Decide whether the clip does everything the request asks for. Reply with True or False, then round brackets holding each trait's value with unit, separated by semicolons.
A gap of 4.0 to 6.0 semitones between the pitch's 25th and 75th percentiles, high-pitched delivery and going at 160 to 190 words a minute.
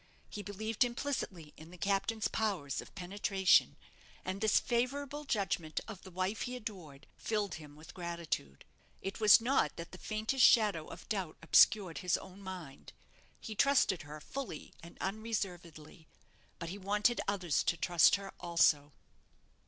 False (4.5 semitones; 195 Hz; 150 wpm)